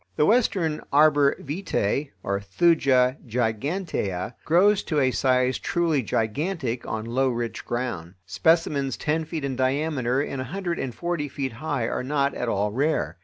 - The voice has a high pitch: No, low, 135 Hz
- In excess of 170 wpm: No, average, 150 wpm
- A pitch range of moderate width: Yes, average, 4.9 semitones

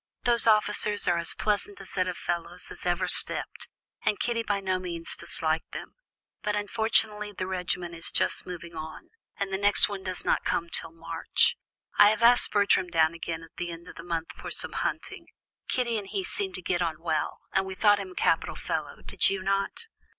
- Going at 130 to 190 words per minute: No, fast, 205 wpm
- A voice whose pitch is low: No, high, 190 Hz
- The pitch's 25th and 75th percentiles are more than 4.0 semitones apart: No, average, 3.5 semitones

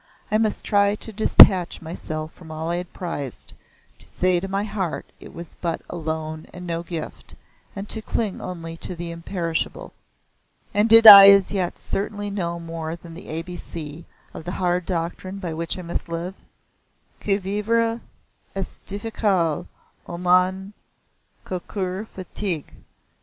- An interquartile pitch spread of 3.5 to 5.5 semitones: No, average, 3.1 semitones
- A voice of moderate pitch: Yes, medium, 180 Hz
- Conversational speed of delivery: Yes, average, 160 wpm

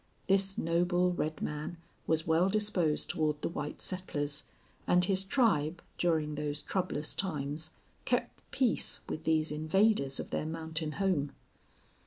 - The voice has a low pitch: No, medium, 160 Hz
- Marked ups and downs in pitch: No, average, 3.6 semitones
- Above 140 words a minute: No, slow, 135 wpm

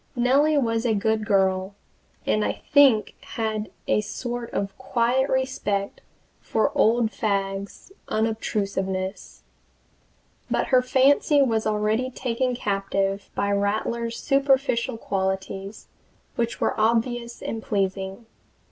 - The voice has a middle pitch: No, high, 220 Hz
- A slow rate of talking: Yes, slow, 110 wpm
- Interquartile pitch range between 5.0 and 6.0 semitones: No, average, 3.6 semitones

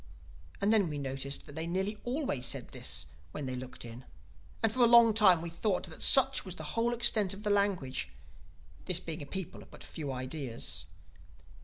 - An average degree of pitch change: No, wide, 7.4 semitones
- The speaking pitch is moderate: Yes, medium, 175 Hz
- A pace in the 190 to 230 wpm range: Yes, average, 195 wpm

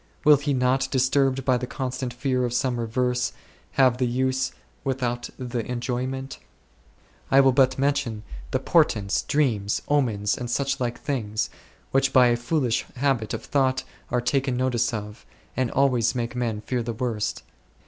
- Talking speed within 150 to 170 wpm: Yes, average, 160 wpm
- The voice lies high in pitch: No, low, 125 Hz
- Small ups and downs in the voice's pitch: Yes, narrow, 2.0 semitones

